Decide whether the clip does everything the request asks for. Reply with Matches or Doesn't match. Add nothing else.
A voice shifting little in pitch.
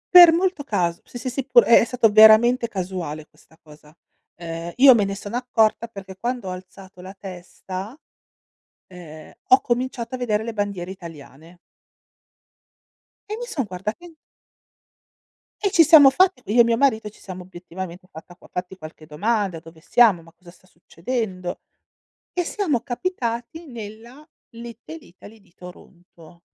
Doesn't match